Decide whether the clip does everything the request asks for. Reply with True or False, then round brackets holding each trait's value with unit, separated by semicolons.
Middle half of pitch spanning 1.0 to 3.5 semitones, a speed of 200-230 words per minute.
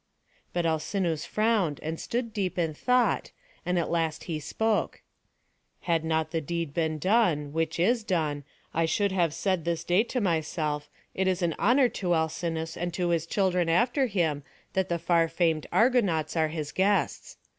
False (3.2 semitones; 175 wpm)